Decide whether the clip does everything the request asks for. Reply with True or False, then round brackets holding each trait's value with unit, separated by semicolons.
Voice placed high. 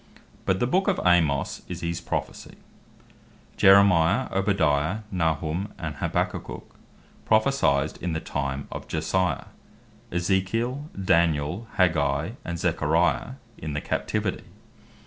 False (85 Hz)